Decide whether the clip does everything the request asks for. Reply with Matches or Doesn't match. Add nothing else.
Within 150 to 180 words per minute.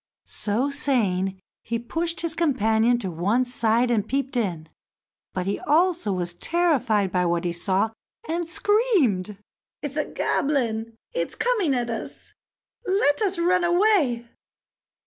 Doesn't match